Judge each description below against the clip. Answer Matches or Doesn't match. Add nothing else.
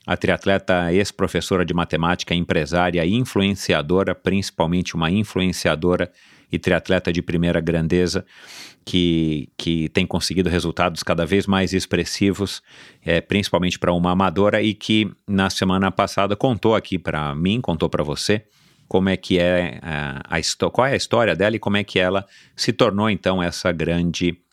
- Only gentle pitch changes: Matches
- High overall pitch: Doesn't match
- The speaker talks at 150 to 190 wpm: Matches